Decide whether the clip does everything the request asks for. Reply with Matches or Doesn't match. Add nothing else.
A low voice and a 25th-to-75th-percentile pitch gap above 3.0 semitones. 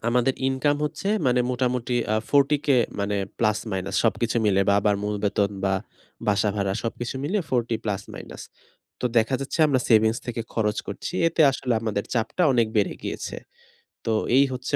Matches